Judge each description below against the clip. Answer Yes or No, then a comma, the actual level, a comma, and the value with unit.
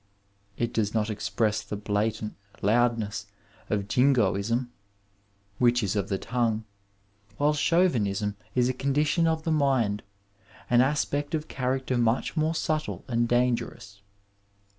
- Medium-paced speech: No, slow, 130 wpm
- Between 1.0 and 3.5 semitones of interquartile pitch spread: No, average, 4.5 semitones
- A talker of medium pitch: No, low, 120 Hz